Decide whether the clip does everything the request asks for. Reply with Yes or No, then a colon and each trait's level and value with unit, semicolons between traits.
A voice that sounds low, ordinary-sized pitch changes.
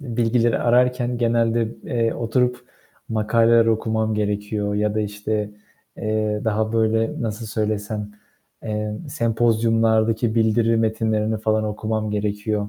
No: low, 110 Hz; narrow, 1.3 semitones